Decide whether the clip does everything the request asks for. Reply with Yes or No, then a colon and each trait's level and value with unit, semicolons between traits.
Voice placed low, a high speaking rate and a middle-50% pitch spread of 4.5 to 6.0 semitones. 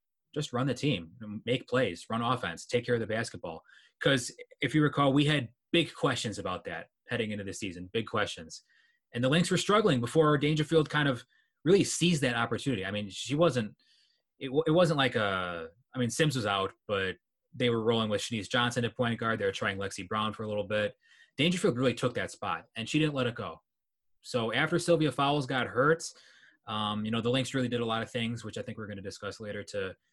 Yes: low, 120 Hz; fast, 225 wpm; average, 5.2 semitones